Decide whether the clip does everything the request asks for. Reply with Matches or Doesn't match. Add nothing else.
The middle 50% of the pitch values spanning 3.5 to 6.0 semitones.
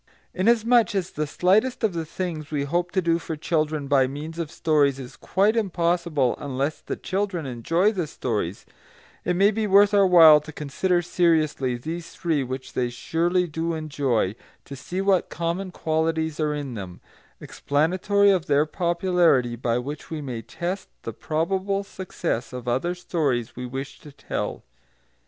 Matches